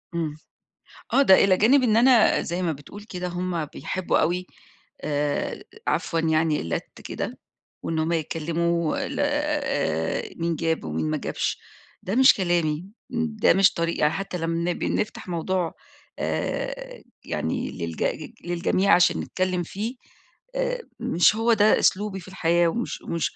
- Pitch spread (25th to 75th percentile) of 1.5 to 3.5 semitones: No, average, 4.0 semitones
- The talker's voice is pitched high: No, medium, 175 Hz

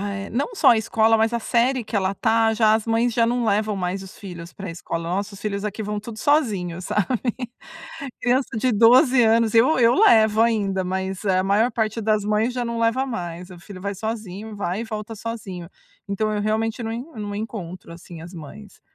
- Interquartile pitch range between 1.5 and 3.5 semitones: Yes, average, 2.9 semitones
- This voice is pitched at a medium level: No, high, 215 Hz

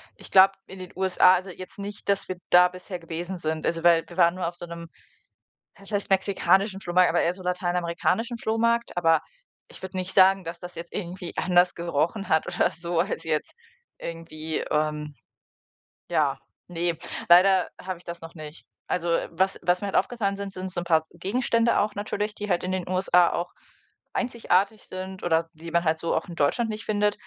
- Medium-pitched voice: Yes, medium, 180 Hz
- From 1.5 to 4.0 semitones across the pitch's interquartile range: Yes, narrow, 2.4 semitones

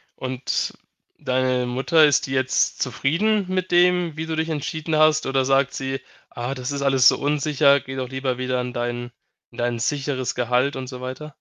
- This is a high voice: No, low, 135 Hz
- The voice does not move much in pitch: No, average, 3.1 semitones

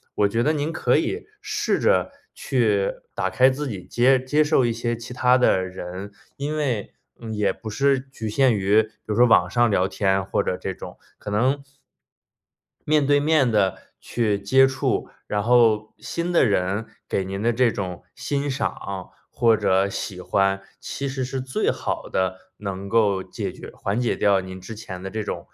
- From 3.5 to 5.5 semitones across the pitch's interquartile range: Yes, average, 5.0 semitones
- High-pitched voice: No, low, 115 Hz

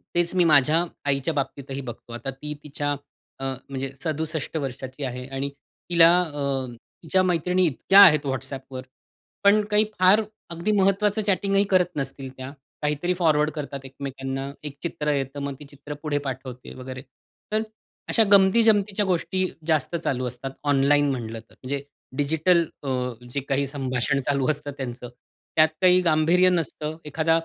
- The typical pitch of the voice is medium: Yes, medium, 145 Hz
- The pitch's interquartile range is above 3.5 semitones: Yes, average, 4.4 semitones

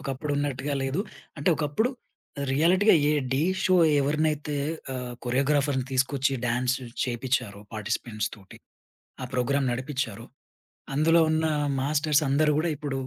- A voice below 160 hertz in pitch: Yes, medium, 140 Hz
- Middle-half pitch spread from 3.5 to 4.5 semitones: No, average, 3.0 semitones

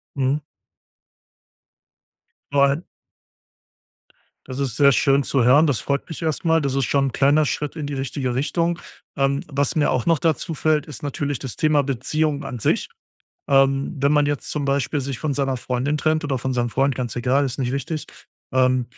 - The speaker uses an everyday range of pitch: No, narrow, 2.1 semitones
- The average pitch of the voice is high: No, medium, 140 Hz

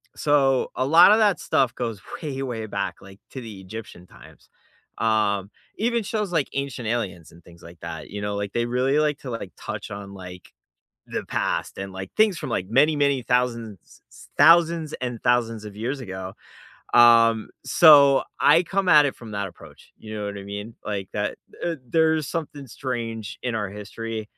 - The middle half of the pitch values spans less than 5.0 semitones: No, wide, 5.6 semitones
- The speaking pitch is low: Yes, low, 115 Hz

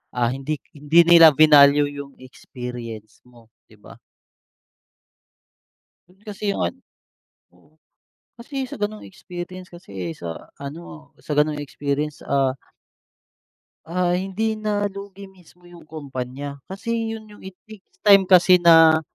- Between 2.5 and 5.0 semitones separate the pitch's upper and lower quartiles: No, wide, 5.6 semitones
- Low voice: No, medium, 165 Hz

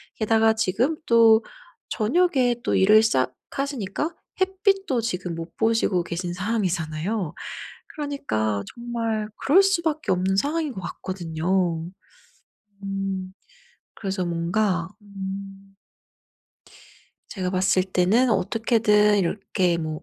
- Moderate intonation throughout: Yes, average, 4.4 semitones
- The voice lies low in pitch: No, high, 200 Hz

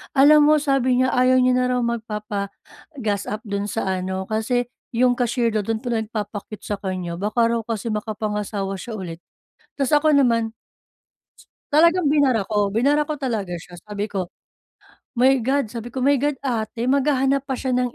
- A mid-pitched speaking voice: No, high, 235 Hz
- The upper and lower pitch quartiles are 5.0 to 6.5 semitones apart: No, average, 4.2 semitones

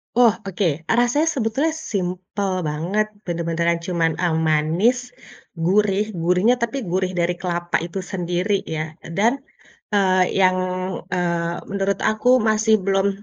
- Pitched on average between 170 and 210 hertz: Yes, high, 190 Hz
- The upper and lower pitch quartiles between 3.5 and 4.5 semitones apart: Yes, average, 4.0 semitones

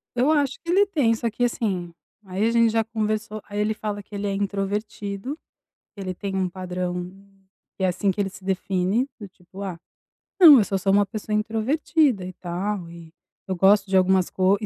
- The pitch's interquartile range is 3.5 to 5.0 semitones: No, average, 2.9 semitones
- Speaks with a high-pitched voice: Yes, high, 200 Hz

